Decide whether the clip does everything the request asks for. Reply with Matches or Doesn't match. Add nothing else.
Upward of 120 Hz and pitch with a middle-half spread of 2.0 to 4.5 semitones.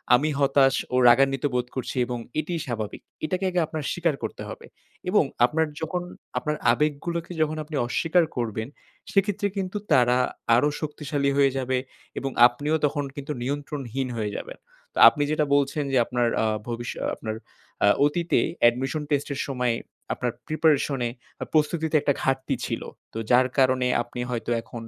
Matches